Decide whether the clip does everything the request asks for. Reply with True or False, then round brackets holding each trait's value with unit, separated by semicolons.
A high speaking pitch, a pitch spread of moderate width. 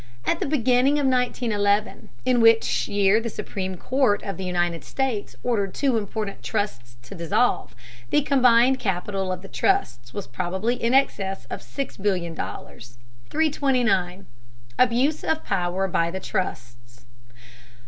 False (205 Hz; 5.8 semitones)